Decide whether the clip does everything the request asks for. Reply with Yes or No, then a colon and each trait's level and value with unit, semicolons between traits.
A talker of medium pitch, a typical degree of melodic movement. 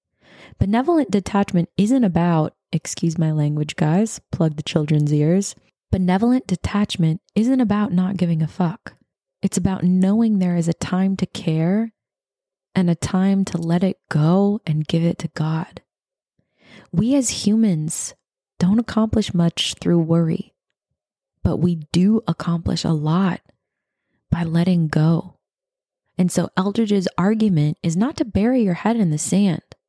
Yes: medium, 180 Hz; average, 3.6 semitones